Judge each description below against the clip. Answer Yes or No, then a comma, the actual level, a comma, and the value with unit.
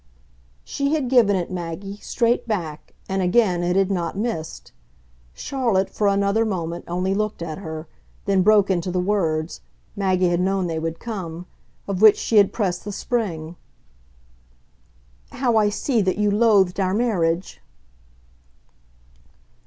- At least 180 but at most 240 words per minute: No, average, 145 wpm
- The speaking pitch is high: Yes, high, 195 Hz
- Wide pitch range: No, average, 3.4 semitones